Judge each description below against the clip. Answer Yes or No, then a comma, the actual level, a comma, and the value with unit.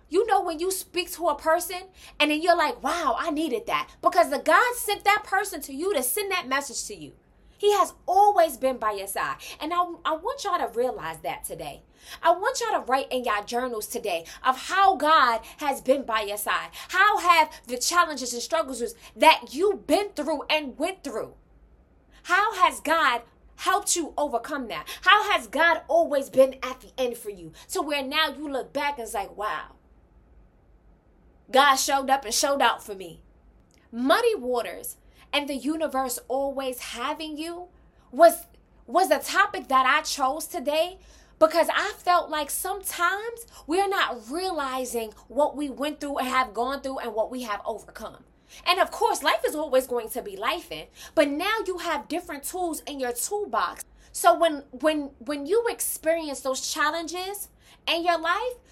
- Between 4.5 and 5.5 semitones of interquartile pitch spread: Yes, average, 5.2 semitones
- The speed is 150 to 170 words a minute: No, average, 185 wpm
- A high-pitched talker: Yes, very high, 310 Hz